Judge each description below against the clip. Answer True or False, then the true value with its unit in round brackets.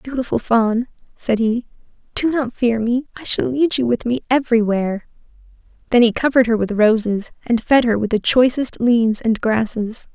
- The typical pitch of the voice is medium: False (235 Hz)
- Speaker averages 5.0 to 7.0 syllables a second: True (5.1 syllables/s)